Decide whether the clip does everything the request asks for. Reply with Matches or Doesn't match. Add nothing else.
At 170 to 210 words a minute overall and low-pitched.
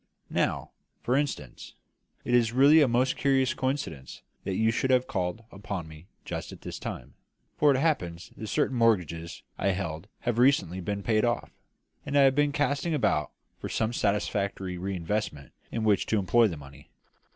Matches